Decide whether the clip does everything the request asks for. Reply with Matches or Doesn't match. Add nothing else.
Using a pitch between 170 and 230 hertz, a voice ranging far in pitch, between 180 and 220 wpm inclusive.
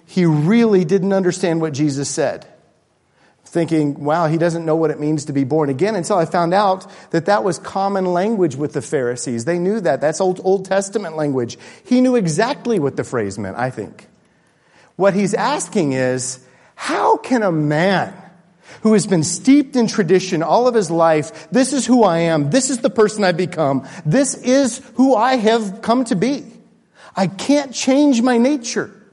Matches